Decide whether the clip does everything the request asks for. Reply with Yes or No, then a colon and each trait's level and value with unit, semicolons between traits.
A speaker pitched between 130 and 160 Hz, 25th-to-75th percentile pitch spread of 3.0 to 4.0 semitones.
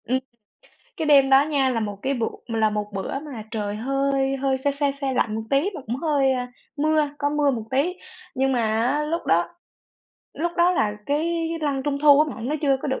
No: very high, 275 Hz; average, 3.5 semitones